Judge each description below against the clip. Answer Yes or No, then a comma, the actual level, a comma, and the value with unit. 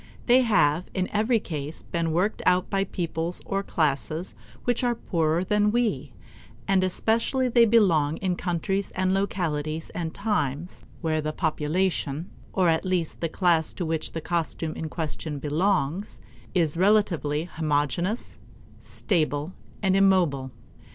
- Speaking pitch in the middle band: Yes, medium, 175 Hz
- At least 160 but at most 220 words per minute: No, average, 140 wpm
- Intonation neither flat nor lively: Yes, average, 4.0 semitones